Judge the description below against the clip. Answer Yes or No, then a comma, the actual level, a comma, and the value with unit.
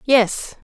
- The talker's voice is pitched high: Yes, high, 240 Hz